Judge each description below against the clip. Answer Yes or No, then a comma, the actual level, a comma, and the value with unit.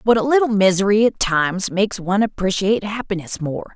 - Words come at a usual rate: Yes, average, 175 wpm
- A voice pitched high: Yes, high, 200 Hz